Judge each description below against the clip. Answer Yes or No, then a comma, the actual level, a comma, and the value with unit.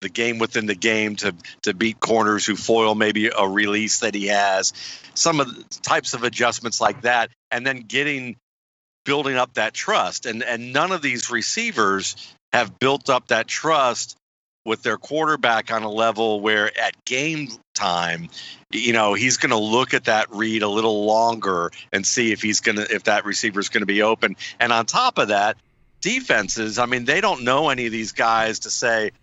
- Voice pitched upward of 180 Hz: No, low, 115 Hz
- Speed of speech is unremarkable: Yes, average, 195 wpm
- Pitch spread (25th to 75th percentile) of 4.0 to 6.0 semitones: No, average, 2.8 semitones